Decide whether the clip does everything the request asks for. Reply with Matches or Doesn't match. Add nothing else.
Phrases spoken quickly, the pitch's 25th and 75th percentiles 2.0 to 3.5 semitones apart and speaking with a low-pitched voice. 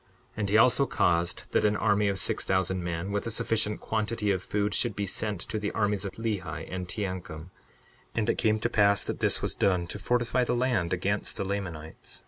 Matches